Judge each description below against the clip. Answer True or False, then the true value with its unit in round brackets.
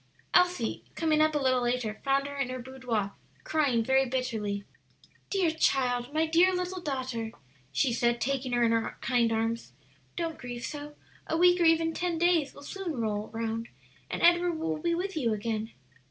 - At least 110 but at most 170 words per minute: False (180 wpm)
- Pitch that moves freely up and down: True (5.8 semitones)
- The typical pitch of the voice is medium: False (265 Hz)